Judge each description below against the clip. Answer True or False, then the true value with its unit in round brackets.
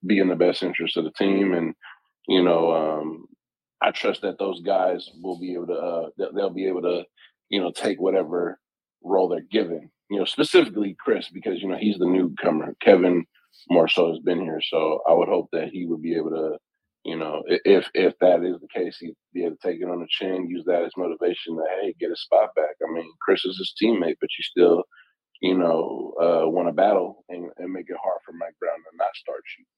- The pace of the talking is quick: True (230 wpm)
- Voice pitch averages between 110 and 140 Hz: False (90 Hz)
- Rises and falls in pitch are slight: False (3.2 semitones)